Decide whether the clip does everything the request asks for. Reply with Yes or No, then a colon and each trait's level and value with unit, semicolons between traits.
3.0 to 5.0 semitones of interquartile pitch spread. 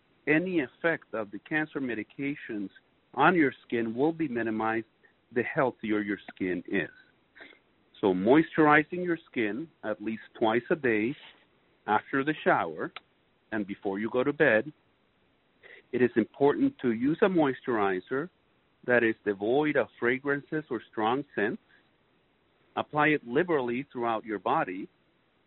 No: wide, 5.6 semitones